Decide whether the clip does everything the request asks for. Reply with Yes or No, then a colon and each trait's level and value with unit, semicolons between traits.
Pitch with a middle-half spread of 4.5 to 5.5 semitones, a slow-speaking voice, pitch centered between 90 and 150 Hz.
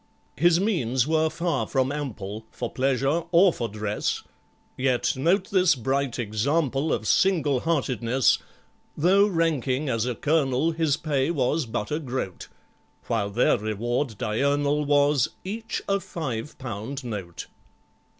Yes: average, 5.2 semitones; slow, 130 wpm; low, 135 Hz